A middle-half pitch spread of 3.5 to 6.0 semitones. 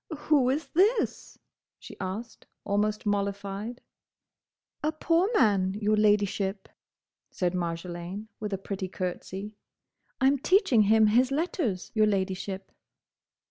Yes: average, 4.7 semitones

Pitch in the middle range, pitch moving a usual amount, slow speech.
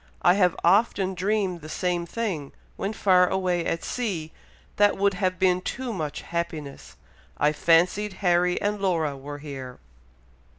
No: medium, 180 Hz; average, 3.3 semitones; average, 145 wpm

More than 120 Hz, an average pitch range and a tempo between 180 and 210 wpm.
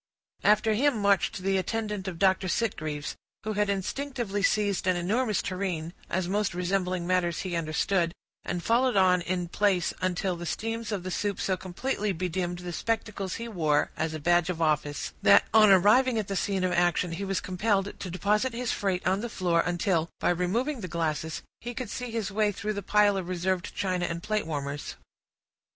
Yes: high, 190 Hz; average, 3.2 semitones; average, 190 wpm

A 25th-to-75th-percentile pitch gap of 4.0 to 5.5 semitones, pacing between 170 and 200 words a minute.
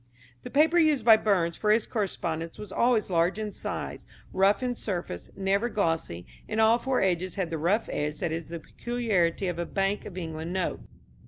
Yes: average, 4.7 semitones; average, 190 wpm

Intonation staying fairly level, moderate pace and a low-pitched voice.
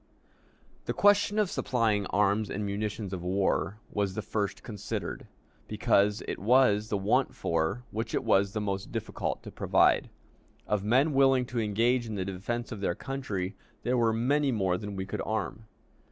No: average, 3.5 semitones; average, 170 wpm; low, 105 Hz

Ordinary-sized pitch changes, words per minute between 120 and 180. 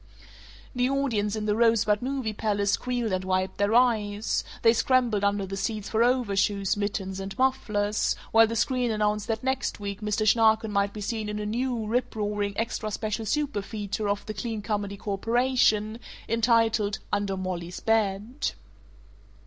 No: narrow, 2.2 semitones; average, 155 wpm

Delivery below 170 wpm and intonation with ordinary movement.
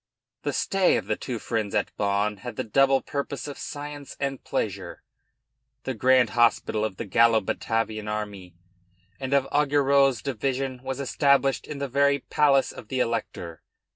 Yes: average, 160 wpm; average, 4.1 semitones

